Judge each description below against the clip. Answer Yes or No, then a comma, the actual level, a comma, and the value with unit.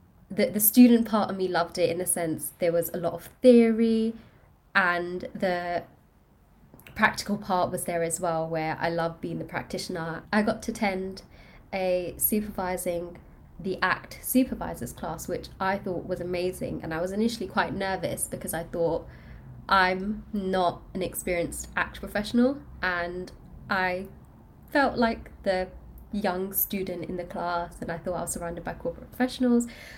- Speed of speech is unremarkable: Yes, average, 160 wpm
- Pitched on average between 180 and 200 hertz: Yes, medium, 185 Hz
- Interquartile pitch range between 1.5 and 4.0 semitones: Yes, average, 3.4 semitones